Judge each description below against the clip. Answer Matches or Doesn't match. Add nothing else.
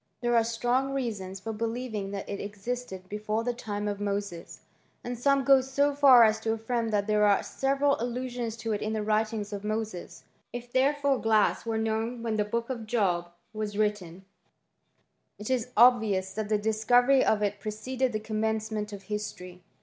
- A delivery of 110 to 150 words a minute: Doesn't match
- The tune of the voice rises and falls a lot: Doesn't match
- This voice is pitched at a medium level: Doesn't match